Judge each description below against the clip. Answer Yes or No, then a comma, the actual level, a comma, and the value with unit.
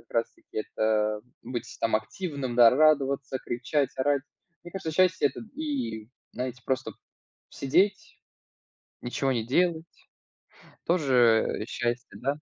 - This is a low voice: Yes, low, 130 Hz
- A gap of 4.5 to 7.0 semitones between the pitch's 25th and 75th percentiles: Yes, average, 4.9 semitones